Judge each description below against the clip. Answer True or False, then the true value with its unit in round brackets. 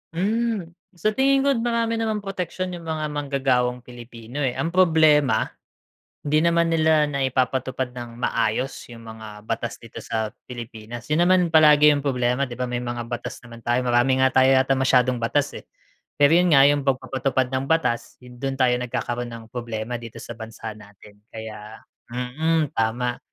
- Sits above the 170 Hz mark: False (130 Hz)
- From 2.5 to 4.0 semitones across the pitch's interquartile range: False (4.7 semitones)